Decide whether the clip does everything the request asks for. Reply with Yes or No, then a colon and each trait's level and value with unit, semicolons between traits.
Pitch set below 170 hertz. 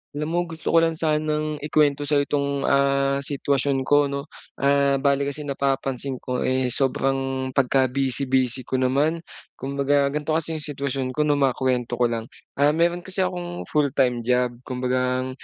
Yes: medium, 140 Hz